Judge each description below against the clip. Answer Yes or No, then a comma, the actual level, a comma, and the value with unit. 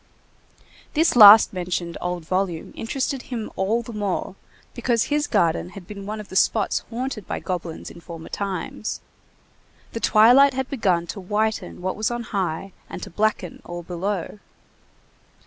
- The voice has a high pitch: Yes, high, 205 Hz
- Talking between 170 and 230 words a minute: No, average, 155 wpm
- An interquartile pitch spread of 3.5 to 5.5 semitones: Yes, average, 4.2 semitones